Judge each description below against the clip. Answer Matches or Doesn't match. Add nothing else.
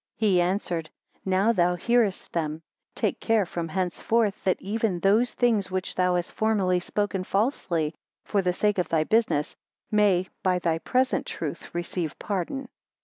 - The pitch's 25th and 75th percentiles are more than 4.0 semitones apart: Doesn't match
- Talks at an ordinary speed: Matches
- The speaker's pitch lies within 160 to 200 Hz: Matches